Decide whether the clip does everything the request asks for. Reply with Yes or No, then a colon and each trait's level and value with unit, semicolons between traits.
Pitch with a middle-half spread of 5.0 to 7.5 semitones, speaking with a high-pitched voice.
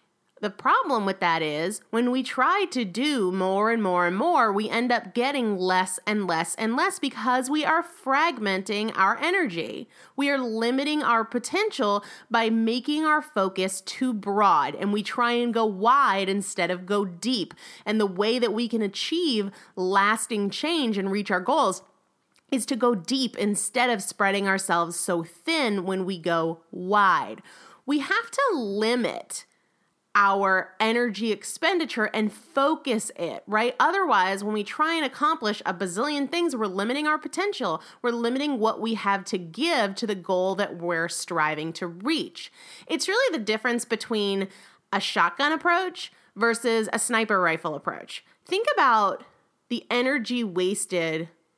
Yes: wide, 5.5 semitones; high, 225 Hz